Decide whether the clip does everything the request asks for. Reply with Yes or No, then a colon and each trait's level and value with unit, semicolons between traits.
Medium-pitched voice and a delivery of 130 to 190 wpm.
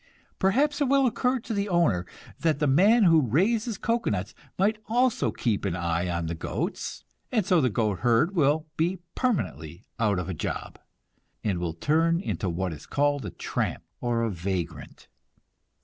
Yes: medium, 145 Hz; average, 165 wpm